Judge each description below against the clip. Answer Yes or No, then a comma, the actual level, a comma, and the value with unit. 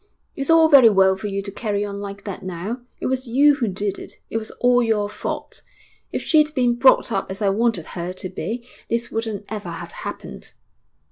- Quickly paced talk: Yes, fast, 210 wpm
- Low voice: No, high, 215 Hz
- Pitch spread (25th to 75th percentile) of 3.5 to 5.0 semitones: Yes, average, 3.8 semitones